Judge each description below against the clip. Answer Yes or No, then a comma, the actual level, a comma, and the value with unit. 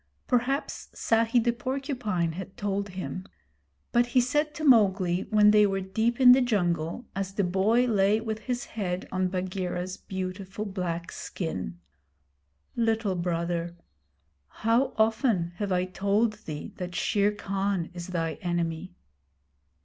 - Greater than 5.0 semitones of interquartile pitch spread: No, average, 4.0 semitones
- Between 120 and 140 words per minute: Yes, slow, 135 wpm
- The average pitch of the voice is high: Yes, high, 195 Hz